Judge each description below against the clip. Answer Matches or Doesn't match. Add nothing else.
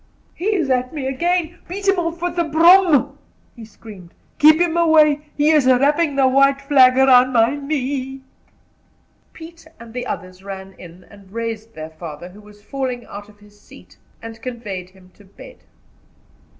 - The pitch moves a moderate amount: Doesn't match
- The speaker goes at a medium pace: Matches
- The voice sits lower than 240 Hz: Doesn't match